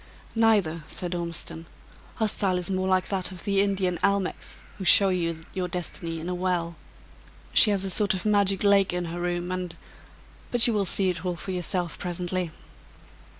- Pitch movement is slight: Yes, narrow, 2.1 semitones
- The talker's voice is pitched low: No, medium, 185 Hz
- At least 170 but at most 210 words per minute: Yes, average, 185 wpm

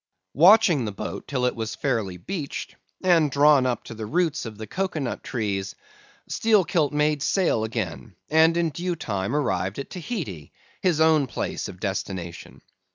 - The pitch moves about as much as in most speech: No, wide, 7.3 semitones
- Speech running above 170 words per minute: No, average, 160 wpm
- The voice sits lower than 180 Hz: Yes, medium, 140 Hz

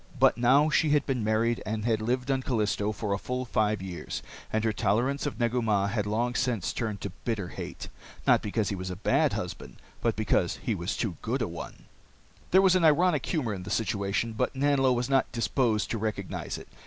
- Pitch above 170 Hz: No, low, 115 Hz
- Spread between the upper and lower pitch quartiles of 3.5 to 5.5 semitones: Yes, average, 3.8 semitones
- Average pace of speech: No, fast, 215 wpm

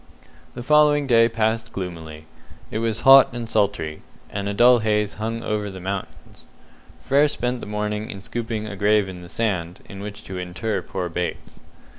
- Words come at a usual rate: Yes, average, 175 wpm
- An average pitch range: Yes, average, 3.3 semitones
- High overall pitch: No, low, 105 Hz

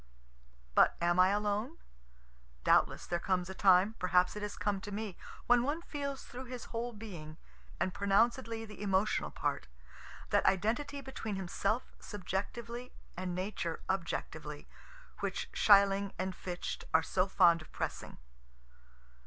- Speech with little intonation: No, average, 3.8 semitones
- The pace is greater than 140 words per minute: No, slow, 135 wpm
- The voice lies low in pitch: No, high, 200 Hz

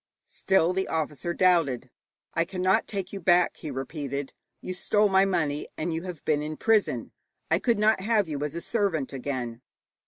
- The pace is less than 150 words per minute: No, average, 180 wpm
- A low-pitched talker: No, medium, 170 Hz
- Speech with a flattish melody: No, average, 4.6 semitones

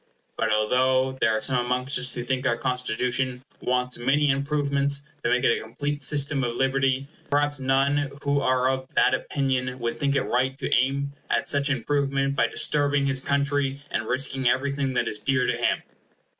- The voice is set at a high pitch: No, low, 135 Hz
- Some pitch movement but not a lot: No, narrow, 1.8 semitones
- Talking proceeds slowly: No, average, 185 wpm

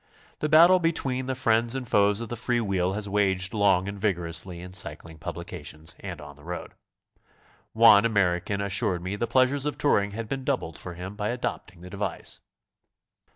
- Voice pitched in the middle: No, low, 100 Hz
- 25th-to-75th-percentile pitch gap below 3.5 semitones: No, average, 4.7 semitones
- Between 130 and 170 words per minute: No, average, 190 wpm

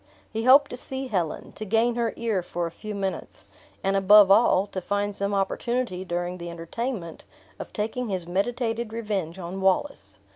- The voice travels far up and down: No, average, 4.0 semitones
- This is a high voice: Yes, high, 205 Hz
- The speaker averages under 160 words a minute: No, average, 175 wpm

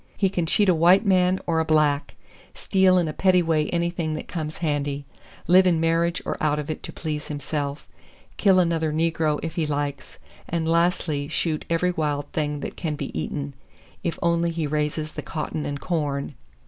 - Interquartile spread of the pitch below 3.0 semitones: Yes, narrow, 2.4 semitones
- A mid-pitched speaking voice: Yes, medium, 160 Hz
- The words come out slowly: No, average, 190 wpm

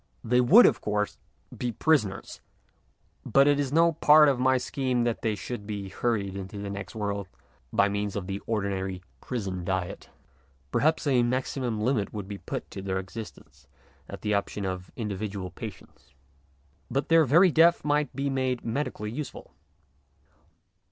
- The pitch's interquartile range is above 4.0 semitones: Yes, average, 5.2 semitones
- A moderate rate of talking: Yes, average, 160 wpm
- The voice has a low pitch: Yes, low, 110 Hz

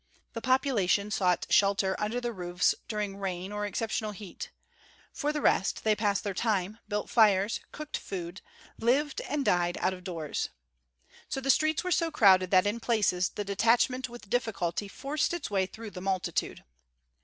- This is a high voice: Yes, high, 210 Hz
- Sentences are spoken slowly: No, average, 165 wpm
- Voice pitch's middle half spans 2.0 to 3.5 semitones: No, average, 4.3 semitones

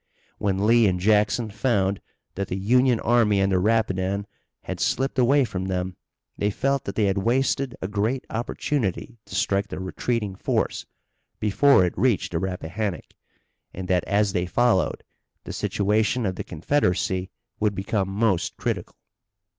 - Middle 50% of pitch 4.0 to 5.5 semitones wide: No, average, 3.6 semitones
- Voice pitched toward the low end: Yes, low, 100 Hz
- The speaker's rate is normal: Yes, average, 155 wpm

